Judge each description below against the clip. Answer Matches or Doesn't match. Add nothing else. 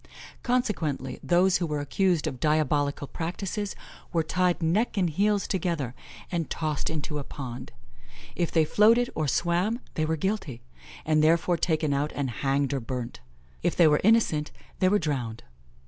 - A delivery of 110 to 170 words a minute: Matches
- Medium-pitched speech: Matches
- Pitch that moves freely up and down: Doesn't match